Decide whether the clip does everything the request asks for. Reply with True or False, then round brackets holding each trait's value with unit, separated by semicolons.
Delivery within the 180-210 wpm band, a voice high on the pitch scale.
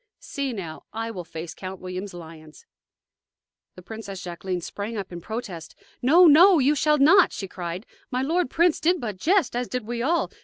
True (185 wpm; 225 Hz)